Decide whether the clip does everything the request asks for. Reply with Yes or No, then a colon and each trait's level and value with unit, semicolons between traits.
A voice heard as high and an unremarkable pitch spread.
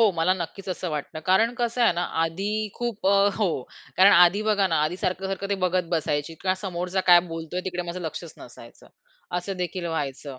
No: medium, 180 Hz; average, 3.0 semitones